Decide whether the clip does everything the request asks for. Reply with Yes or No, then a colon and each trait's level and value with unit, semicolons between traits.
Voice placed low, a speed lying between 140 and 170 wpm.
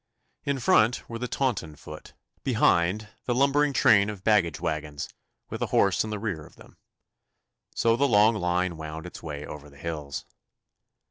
Yes: low, 100 Hz; average, 165 wpm